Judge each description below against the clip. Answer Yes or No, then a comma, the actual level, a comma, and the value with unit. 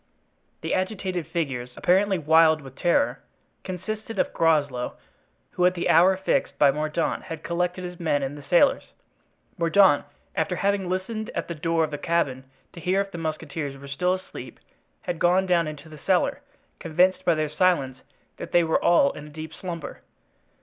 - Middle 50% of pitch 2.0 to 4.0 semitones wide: Yes, average, 3.3 semitones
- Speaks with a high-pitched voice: No, medium, 170 Hz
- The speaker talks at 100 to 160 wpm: No, average, 175 wpm